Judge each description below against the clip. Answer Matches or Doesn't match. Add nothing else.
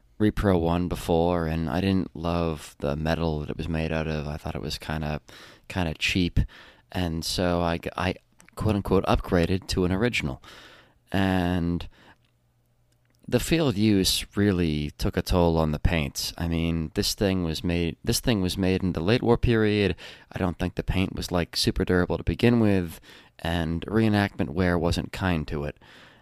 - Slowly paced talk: Doesn't match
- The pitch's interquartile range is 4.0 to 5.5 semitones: Doesn't match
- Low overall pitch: Matches